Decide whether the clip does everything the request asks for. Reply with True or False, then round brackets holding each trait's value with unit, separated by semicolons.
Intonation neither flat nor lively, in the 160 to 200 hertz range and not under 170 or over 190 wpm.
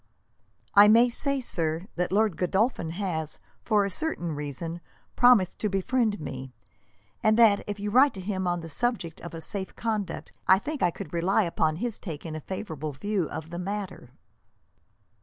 True (4.6 semitones; 190 Hz; 175 wpm)